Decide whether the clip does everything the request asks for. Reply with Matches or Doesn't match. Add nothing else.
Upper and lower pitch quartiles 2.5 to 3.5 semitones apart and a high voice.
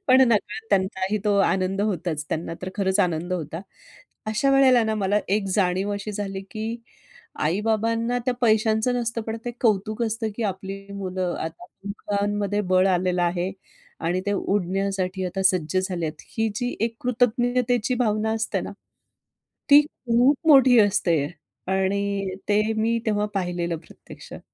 Matches